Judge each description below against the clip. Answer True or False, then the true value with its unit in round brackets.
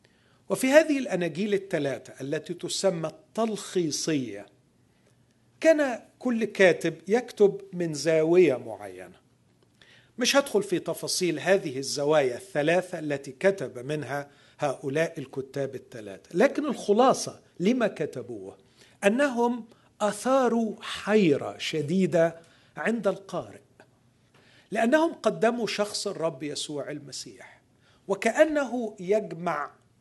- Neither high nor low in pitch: True (175 Hz)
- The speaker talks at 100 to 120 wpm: False (90 wpm)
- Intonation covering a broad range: True (6.8 semitones)